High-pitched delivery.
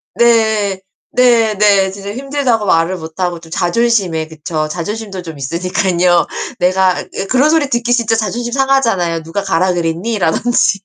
Yes: high, 195 Hz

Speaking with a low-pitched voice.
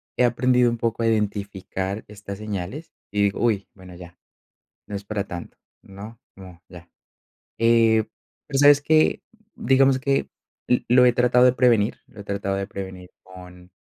Yes: low, 105 Hz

